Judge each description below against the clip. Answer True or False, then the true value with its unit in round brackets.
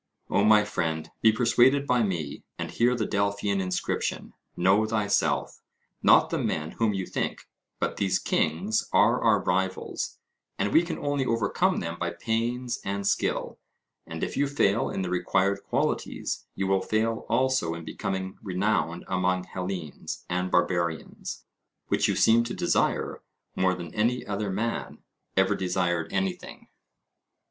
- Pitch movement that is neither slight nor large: True (3.7 semitones)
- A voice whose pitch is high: False (100 Hz)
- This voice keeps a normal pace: True (150 wpm)